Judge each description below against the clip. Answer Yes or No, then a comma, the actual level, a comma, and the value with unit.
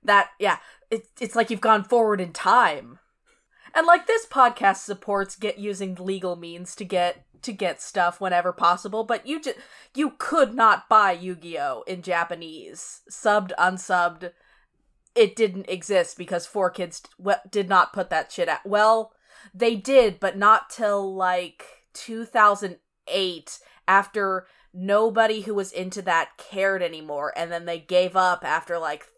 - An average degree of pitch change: Yes, average, 3.7 semitones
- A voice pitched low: No, high, 195 Hz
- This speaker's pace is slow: No, average, 155 wpm